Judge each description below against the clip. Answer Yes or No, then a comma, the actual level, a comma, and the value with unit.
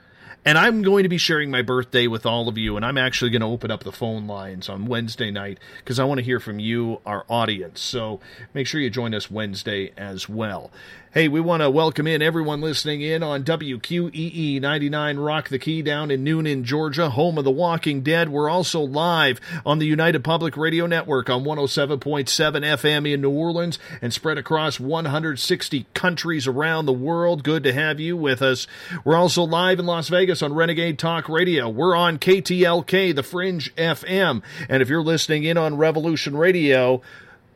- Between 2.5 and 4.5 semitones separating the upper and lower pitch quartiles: Yes, average, 4.2 semitones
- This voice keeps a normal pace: Yes, average, 190 wpm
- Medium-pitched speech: Yes, medium, 150 Hz